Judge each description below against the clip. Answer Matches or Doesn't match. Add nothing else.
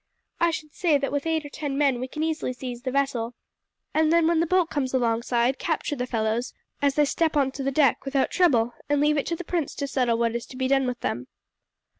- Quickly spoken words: Matches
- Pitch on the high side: Matches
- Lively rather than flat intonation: Doesn't match